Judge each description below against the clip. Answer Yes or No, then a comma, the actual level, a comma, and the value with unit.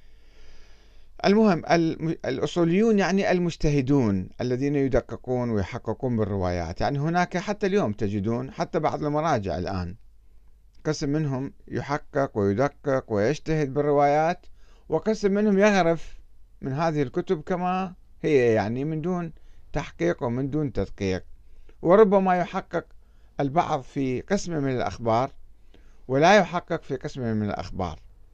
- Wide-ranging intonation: Yes, wide, 7.4 semitones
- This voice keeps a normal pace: Yes, average, 110 wpm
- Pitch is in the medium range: Yes, medium, 145 Hz